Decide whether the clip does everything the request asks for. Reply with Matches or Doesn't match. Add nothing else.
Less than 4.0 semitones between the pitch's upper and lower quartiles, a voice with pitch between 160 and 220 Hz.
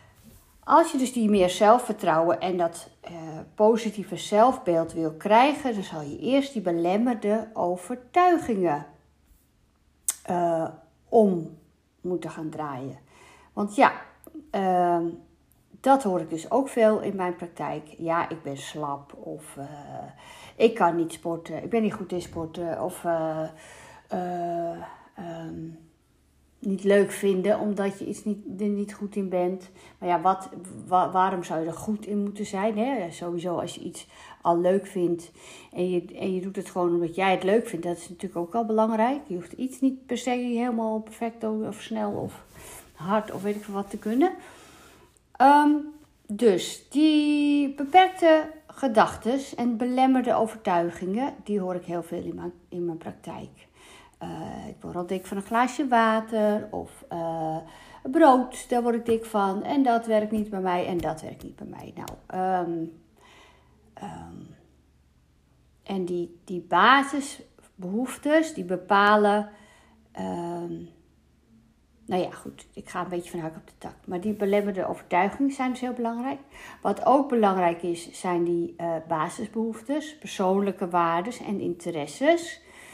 Doesn't match